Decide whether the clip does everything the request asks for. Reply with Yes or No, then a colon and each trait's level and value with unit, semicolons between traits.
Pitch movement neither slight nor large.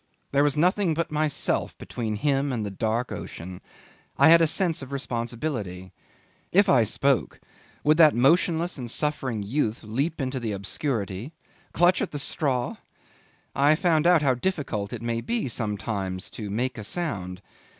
No: wide, 6.1 semitones